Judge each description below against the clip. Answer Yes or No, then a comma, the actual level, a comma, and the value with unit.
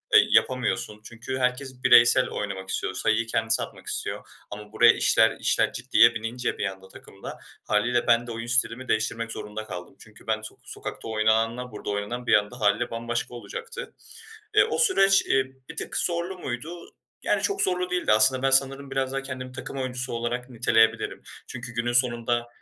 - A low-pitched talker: Yes, low, 120 Hz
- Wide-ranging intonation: No, average, 2.8 semitones